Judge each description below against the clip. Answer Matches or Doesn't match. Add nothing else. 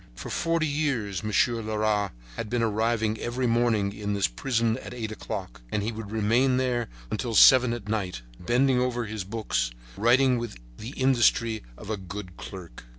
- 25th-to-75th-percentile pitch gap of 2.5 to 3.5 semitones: Matches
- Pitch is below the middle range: Matches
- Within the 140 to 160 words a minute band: Doesn't match